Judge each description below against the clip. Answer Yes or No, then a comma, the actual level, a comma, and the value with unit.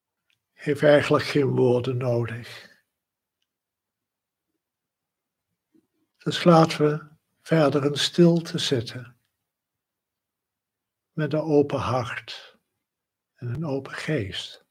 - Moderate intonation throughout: Yes, average, 3.8 semitones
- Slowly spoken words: Yes, slow, 80 wpm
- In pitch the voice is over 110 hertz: Yes, medium, 140 Hz